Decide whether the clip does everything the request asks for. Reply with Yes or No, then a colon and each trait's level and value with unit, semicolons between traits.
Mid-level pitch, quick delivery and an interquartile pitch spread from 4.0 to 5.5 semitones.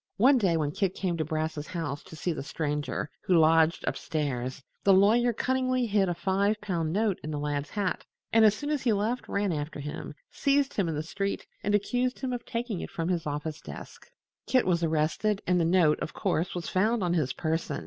Yes: medium, 180 Hz; fast, 220 wpm; average, 5.2 semitones